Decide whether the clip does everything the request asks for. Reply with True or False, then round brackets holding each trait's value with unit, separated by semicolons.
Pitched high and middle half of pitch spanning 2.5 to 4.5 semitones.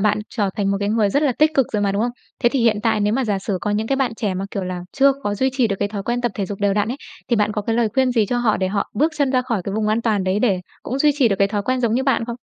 True (220 Hz; 3.7 semitones)